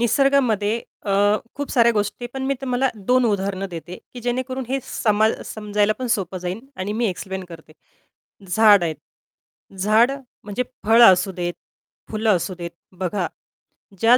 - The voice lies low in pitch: No, high, 215 Hz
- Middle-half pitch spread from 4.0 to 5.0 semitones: Yes, average, 4.3 semitones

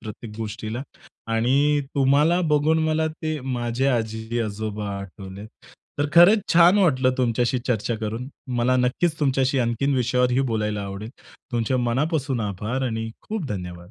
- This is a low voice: Yes, low, 125 Hz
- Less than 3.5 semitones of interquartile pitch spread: No, average, 4.3 semitones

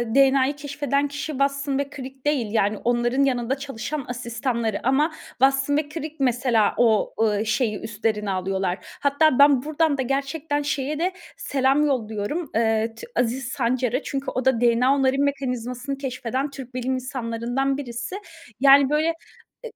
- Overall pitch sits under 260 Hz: No, very high, 265 Hz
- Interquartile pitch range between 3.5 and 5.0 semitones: No, average, 3.1 semitones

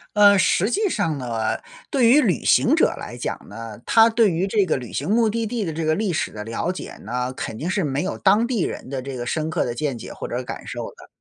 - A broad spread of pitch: Yes, wide, 8.9 semitones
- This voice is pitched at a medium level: Yes, medium, 165 Hz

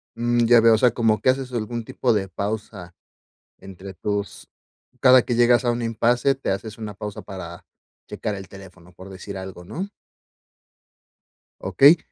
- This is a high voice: No, low, 110 Hz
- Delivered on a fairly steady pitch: No, average, 3.7 semitones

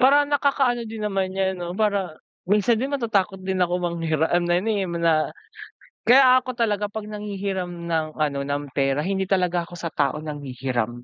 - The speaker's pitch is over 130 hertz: Yes, high, 190 Hz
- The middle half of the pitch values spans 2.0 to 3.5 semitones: No, average, 4.7 semitones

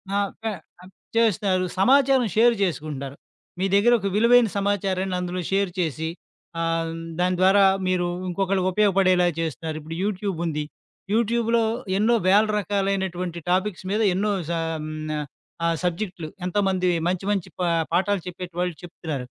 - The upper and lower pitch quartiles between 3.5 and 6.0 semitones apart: No, average, 2.7 semitones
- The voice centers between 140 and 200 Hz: Yes, medium, 185 Hz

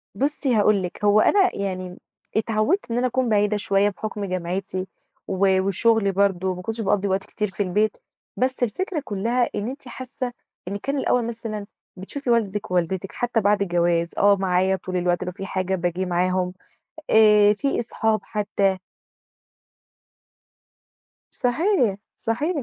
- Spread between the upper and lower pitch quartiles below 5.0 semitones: Yes, average, 3.6 semitones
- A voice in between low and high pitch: No, high, 205 Hz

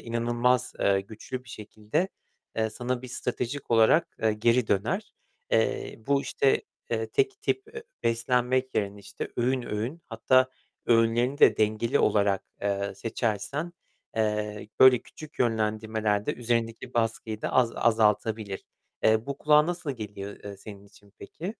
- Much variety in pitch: No, average, 3.2 semitones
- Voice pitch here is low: Yes, low, 115 Hz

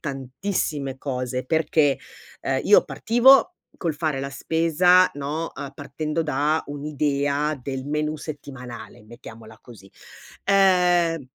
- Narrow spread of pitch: No, average, 3.6 semitones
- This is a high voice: No, medium, 145 Hz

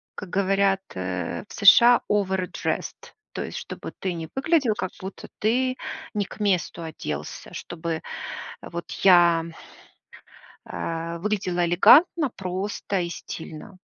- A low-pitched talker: No, high, 190 Hz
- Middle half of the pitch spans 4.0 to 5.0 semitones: No, average, 3.5 semitones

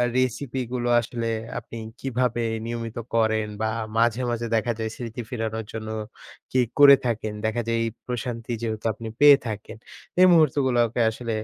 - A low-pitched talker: Yes, low, 115 Hz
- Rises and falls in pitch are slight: Yes, narrow, 1.9 semitones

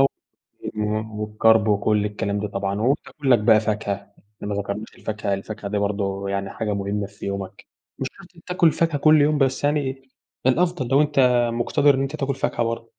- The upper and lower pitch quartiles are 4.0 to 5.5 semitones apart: Yes, average, 5.2 semitones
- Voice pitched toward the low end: Yes, low, 110 Hz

